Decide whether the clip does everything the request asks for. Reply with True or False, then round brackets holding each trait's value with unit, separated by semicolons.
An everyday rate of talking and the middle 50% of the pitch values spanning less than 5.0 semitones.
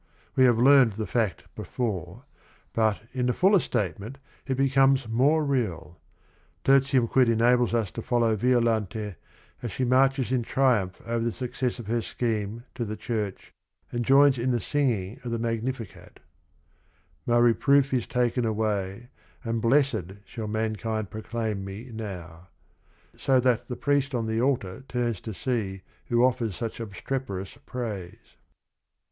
True (155 wpm; 3.0 semitones)